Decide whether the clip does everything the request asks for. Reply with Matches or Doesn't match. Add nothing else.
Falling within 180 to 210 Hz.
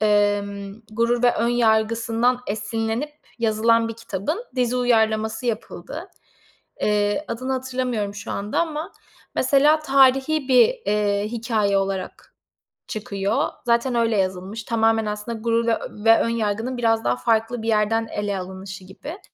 Doesn't match